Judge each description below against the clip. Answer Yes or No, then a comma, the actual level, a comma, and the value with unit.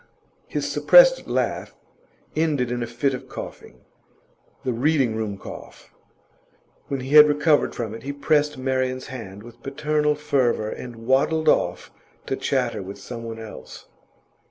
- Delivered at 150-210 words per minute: No, average, 140 wpm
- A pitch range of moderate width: Yes, average, 4.1 semitones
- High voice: No, low, 130 Hz